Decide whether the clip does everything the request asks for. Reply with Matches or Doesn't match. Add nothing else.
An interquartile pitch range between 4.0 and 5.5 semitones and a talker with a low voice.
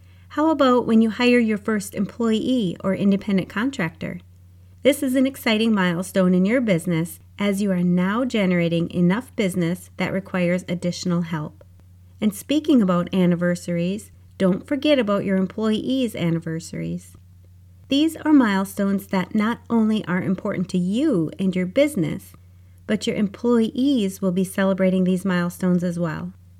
Doesn't match